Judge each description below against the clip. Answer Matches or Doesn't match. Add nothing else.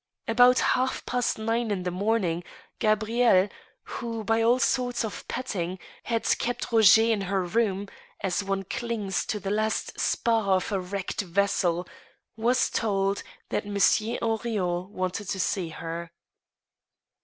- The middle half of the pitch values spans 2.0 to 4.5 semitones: Matches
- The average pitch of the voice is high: Matches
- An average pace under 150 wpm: Matches